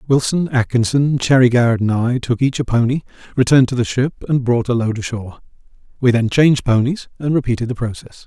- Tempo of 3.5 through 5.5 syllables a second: No, 6.1 syllables/s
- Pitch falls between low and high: No, low, 125 Hz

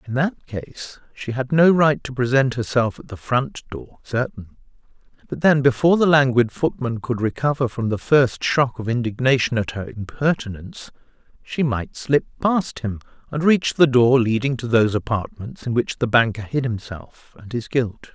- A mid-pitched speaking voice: No, low, 125 Hz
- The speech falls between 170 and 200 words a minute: Yes, average, 180 wpm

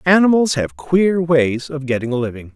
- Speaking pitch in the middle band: Yes, medium, 145 Hz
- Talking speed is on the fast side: No, average, 190 wpm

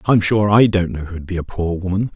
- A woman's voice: No, male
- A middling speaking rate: No, fast, 280 wpm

